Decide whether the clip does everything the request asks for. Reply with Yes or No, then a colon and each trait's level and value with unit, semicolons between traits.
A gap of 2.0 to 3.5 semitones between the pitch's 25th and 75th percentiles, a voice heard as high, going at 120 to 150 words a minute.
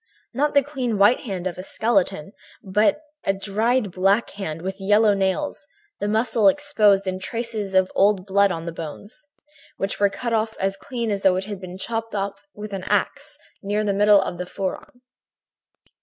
No: average, 2.8 semitones; high, 200 Hz; average, 185 wpm